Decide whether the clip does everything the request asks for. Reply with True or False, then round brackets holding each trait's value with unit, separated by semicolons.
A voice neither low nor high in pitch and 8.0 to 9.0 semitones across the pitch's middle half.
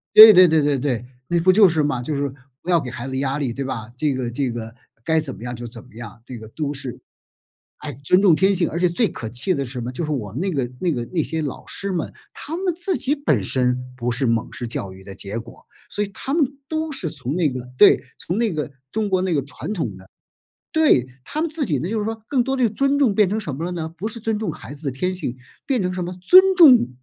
True (155 Hz; 8.5 semitones)